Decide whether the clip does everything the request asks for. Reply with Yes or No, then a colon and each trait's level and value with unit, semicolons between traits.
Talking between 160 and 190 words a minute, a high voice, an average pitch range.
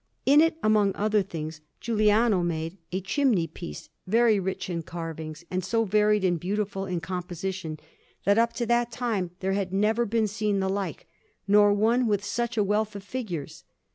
Yes: average, 175 wpm; high, 200 Hz; average, 3.2 semitones